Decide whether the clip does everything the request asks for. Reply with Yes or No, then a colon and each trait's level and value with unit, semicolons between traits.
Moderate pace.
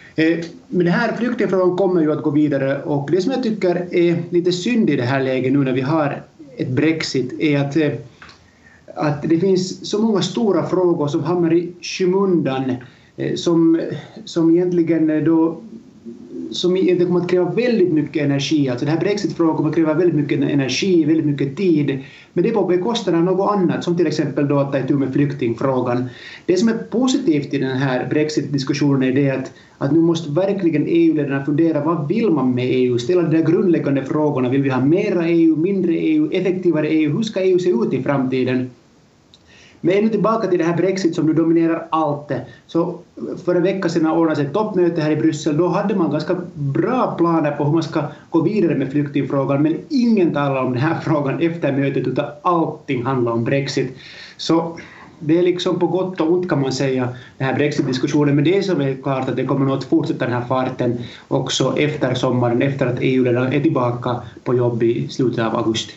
No: fast, 200 wpm